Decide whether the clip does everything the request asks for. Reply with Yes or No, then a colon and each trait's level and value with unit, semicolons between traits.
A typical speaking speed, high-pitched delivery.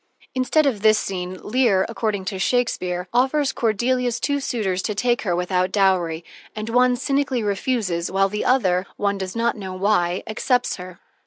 Yes: average, 165 wpm; high, 210 Hz